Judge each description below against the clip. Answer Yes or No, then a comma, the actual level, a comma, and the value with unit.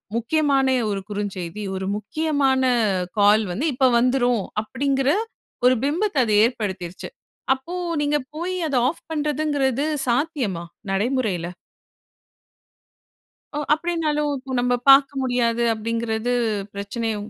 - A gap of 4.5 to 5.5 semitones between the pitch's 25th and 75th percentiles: Yes, average, 4.9 semitones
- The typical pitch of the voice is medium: No, very high, 255 Hz